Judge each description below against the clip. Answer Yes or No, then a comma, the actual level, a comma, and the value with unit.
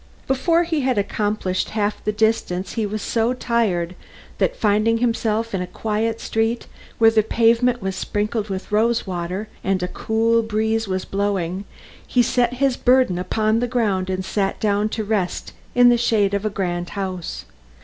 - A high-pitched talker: Yes, high, 215 Hz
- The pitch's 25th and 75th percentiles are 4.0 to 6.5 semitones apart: No, average, 3.0 semitones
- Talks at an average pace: Yes, average, 170 wpm